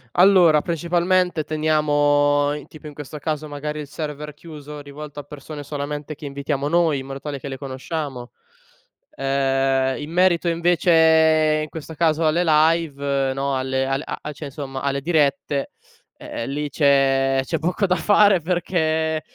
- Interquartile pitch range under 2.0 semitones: No, narrow, 2.5 semitones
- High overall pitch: No, medium, 150 Hz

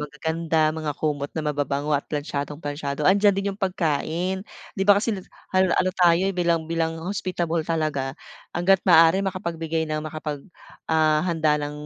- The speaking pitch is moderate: Yes, medium, 160 Hz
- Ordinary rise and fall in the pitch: Yes, average, 3.3 semitones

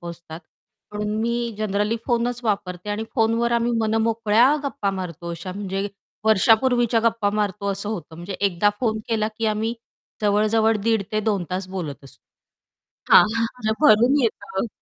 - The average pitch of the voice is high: Yes, high, 215 Hz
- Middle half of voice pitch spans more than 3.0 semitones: No, average, 2.7 semitones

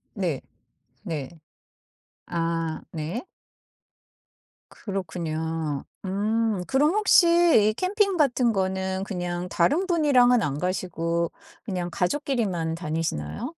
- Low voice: No, high, 190 Hz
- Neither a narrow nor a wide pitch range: No, wide, 6.9 semitones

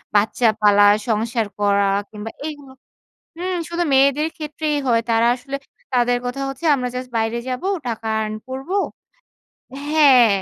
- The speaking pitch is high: Yes, very high, 250 Hz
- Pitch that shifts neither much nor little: Yes, average, 4.0 semitones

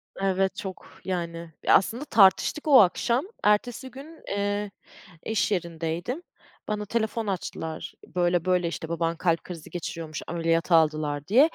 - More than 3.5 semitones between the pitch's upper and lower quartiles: Yes, average, 4.3 semitones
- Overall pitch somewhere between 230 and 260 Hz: No, medium, 185 Hz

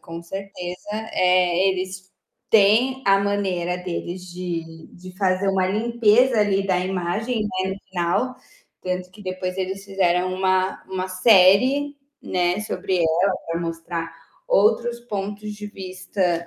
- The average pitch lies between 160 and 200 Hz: Yes, medium, 185 Hz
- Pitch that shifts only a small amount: Yes, narrow, 2.3 semitones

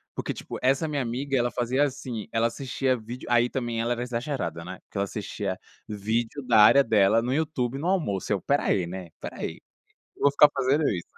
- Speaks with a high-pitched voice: No, low, 120 Hz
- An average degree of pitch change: Yes, average, 4.4 semitones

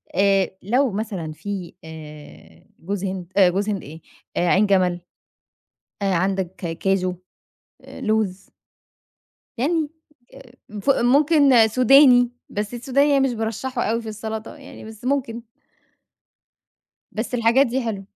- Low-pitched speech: No, high, 215 Hz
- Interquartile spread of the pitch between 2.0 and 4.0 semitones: No, average, 4.7 semitones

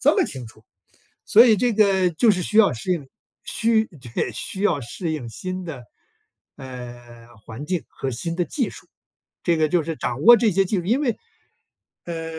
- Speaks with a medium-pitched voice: Yes, medium, 175 Hz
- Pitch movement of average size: No, wide, 7.7 semitones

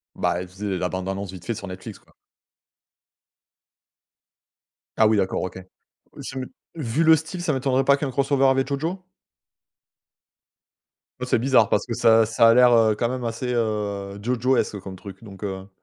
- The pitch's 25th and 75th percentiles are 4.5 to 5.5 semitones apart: Yes, average, 5.1 semitones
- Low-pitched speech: Yes, low, 115 Hz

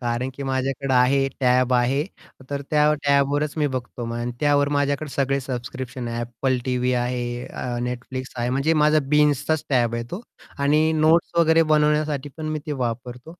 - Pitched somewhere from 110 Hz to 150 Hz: Yes, low, 135 Hz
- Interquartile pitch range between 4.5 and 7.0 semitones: No, average, 3.1 semitones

